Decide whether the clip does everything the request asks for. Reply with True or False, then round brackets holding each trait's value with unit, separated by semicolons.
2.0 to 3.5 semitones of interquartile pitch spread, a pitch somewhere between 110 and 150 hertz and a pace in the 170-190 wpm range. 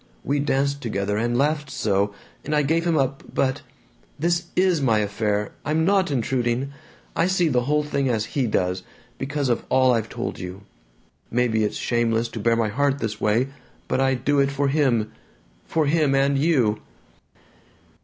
False (4.3 semitones; 135 Hz; 175 wpm)